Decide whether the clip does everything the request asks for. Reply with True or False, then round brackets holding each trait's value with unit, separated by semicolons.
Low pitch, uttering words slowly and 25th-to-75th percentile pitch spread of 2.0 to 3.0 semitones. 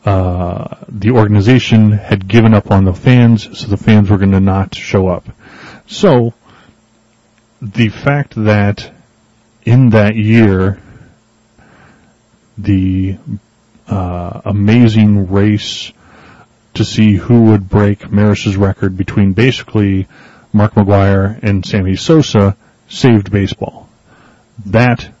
True (105 Hz; 105 wpm; 2.4 semitones)